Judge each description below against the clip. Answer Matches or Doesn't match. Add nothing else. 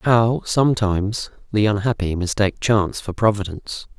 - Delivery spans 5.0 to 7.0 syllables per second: Matches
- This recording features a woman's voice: Doesn't match